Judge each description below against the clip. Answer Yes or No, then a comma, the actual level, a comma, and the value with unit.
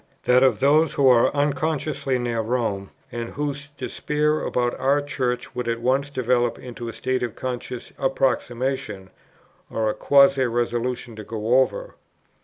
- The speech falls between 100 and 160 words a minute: Yes, average, 155 wpm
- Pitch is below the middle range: Yes, low, 125 Hz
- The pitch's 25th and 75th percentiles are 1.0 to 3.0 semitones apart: Yes, average, 2.7 semitones